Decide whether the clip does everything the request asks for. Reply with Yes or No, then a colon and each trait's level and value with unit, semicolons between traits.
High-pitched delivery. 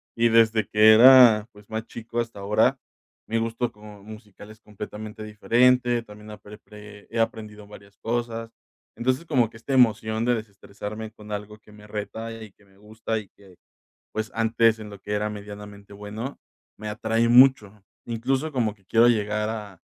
No: low, 110 Hz